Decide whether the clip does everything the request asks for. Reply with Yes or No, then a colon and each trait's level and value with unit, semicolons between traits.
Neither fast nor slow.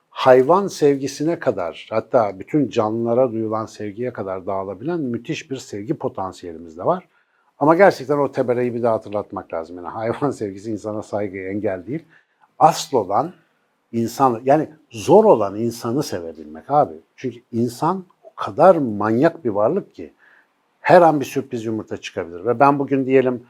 No: fast, 150 wpm